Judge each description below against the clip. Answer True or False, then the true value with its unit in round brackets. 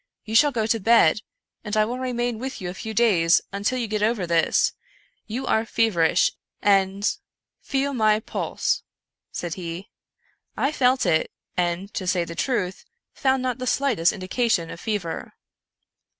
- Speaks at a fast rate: False (170 wpm)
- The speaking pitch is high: True (215 Hz)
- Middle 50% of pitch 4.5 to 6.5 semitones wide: True (5.0 semitones)